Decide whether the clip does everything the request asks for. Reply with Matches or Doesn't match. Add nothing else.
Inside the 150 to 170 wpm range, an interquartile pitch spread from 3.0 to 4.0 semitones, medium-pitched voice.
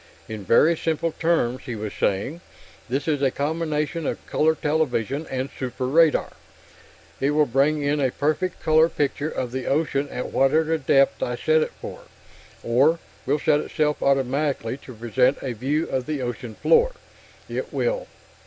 Matches